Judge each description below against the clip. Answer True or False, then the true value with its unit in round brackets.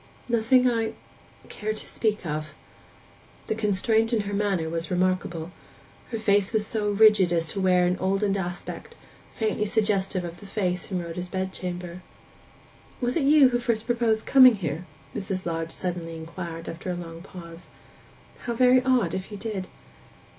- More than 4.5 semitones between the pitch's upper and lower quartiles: False (3.8 semitones)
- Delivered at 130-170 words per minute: True (160 wpm)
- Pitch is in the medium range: False (195 Hz)